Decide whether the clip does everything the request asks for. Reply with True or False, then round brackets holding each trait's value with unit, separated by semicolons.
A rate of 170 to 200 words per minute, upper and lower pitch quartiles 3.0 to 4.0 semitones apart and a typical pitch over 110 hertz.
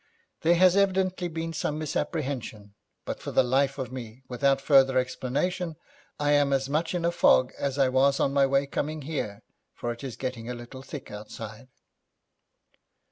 True (175 wpm; 3.6 semitones; 135 Hz)